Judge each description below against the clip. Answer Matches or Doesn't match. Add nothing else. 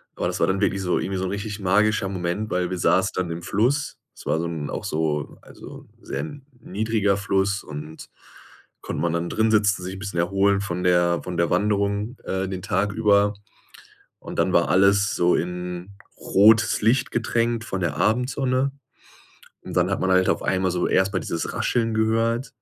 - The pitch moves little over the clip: Doesn't match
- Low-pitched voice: Matches